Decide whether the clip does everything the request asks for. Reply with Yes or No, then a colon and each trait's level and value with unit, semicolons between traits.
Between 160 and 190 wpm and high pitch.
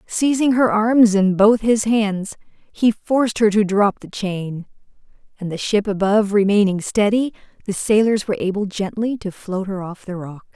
Yes: average, 175 wpm; high, 205 Hz